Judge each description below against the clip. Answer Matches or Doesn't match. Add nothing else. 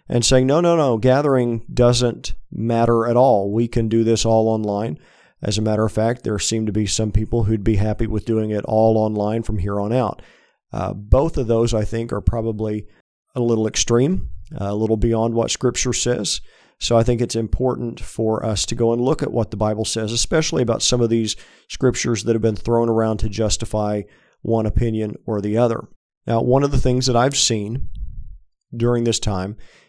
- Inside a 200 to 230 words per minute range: Matches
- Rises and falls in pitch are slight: Matches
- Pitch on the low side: Matches